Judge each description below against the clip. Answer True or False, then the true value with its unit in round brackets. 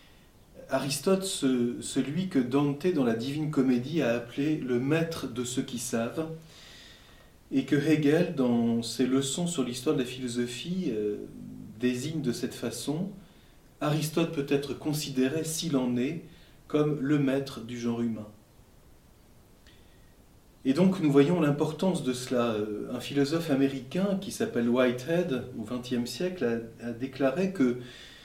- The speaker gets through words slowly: True (140 wpm)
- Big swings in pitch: False (4.1 semitones)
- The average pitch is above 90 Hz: True (135 Hz)